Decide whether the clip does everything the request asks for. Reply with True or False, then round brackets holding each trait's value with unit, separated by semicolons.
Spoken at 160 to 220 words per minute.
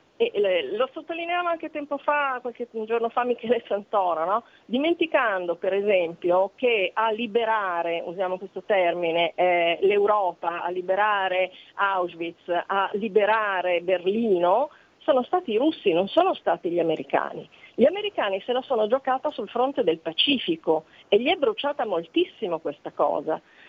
False (135 wpm)